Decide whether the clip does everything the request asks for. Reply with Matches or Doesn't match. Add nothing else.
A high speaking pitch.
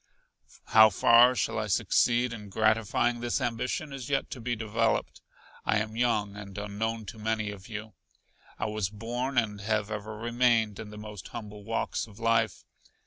Doesn't match